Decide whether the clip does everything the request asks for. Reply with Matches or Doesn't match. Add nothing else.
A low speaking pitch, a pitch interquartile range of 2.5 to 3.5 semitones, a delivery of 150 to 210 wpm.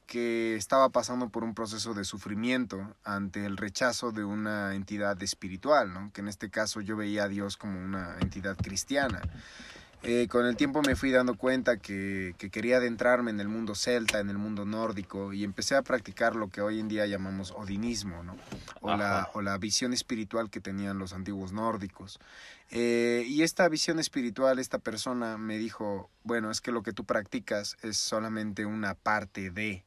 Matches